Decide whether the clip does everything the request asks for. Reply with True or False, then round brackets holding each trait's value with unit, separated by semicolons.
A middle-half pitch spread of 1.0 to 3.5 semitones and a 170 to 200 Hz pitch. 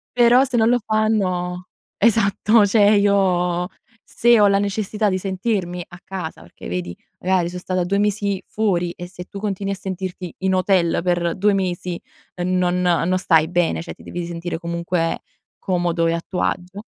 True (2.4 semitones; 185 Hz)